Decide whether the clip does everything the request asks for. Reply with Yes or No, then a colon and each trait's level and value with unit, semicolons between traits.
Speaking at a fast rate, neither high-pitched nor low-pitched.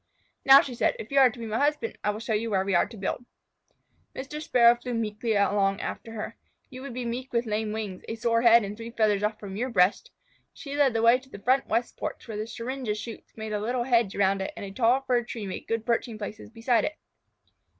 No: fast, 245 wpm; high, 230 Hz